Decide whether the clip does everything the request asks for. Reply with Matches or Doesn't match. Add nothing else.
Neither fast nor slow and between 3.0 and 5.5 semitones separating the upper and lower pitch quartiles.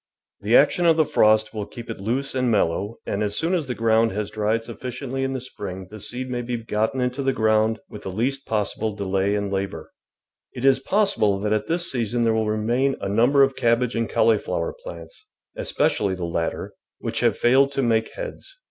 Doesn't match